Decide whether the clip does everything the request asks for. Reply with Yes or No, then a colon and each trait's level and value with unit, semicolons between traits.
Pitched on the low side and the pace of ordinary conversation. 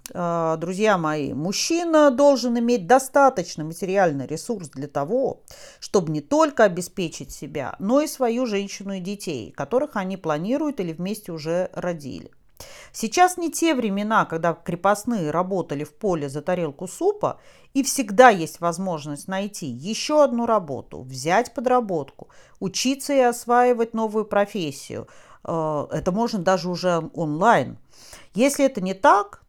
No: high, 195 Hz; average, 130 wpm